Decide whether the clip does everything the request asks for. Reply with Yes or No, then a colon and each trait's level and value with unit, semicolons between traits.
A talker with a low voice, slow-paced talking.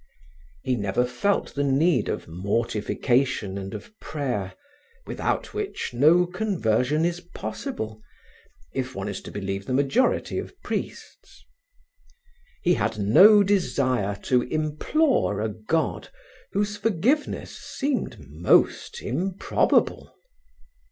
Yes: low, 130 Hz; slow, 110 wpm